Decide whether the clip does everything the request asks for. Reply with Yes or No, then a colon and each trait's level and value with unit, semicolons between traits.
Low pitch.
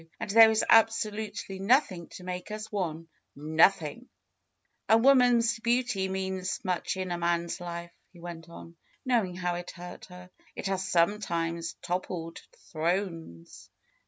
No: medium, 185 Hz